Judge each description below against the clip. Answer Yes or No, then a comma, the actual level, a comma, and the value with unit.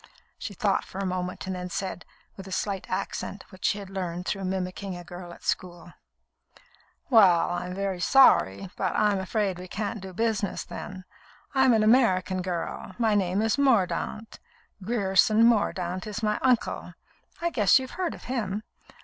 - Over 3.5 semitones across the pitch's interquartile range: No, average, 3.0 semitones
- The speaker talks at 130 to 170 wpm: Yes, average, 165 wpm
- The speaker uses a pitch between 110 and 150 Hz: No, high, 195 Hz